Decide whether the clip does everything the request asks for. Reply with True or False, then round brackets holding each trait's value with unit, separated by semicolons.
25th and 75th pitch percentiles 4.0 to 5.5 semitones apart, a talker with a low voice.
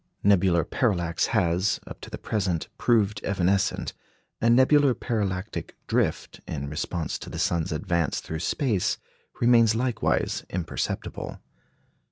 True (5.0 semitones; 100 Hz)